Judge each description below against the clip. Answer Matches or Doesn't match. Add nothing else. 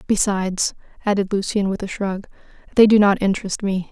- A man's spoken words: Doesn't match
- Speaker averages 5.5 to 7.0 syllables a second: Matches